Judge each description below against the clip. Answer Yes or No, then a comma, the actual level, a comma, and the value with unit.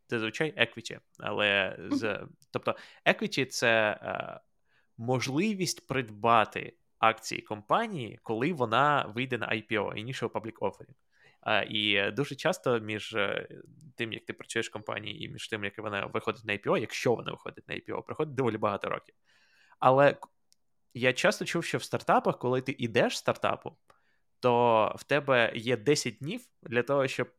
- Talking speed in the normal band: No, fast, 165 wpm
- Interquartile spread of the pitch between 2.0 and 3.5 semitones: No, average, 3.9 semitones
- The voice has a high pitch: No, low, 125 Hz